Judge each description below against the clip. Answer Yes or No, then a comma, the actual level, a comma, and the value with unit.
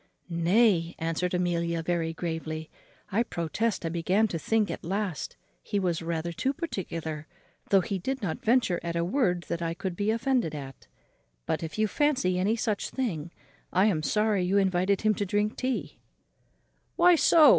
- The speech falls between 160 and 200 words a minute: Yes, average, 170 wpm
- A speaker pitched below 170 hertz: No, medium, 185 Hz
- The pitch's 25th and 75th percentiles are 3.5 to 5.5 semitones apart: Yes, average, 4.4 semitones